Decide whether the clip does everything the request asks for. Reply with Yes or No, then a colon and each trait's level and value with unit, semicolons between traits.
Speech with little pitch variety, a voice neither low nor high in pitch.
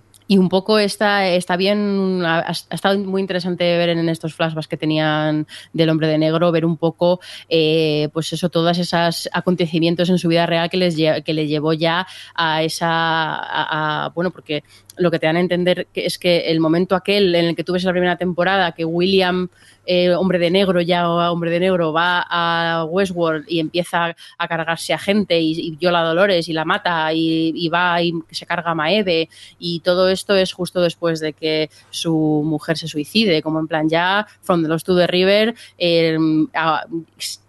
Yes: narrow, 1.9 semitones; medium, 170 Hz